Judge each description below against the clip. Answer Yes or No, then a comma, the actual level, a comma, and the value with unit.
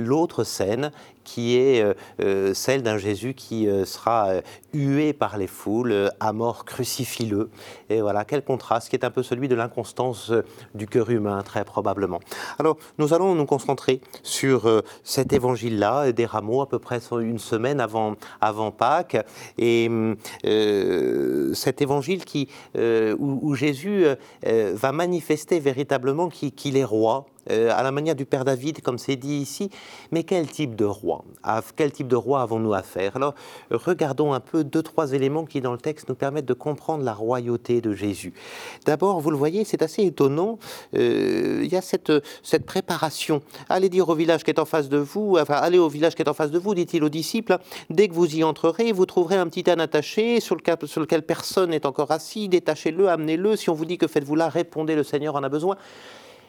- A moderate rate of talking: Yes, average, 185 wpm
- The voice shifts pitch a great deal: Yes, wide, 5.8 semitones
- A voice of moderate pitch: Yes, medium, 145 Hz